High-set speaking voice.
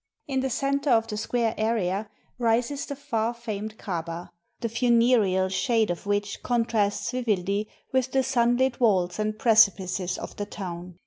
Yes: high, 220 Hz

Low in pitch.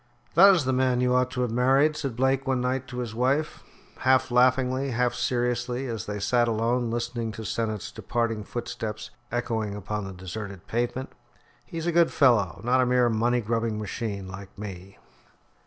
Yes: low, 120 Hz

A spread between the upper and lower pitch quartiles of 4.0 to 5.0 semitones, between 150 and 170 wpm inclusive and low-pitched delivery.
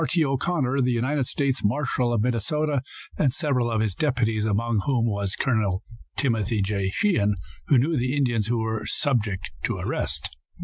Yes: average, 4.5 semitones; average, 165 wpm; low, 120 Hz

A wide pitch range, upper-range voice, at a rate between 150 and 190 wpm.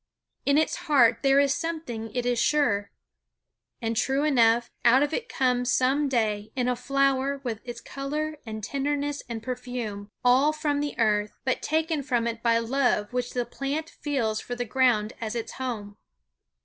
No: average, 3.6 semitones; very high, 250 Hz; average, 170 wpm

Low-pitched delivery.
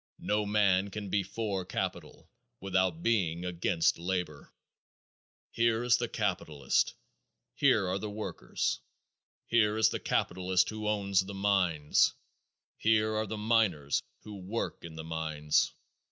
Yes: very low, 95 Hz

